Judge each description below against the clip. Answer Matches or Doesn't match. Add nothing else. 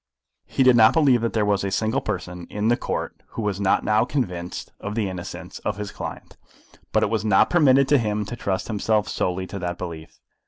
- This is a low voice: Matches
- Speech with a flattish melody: Doesn't match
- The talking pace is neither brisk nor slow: Doesn't match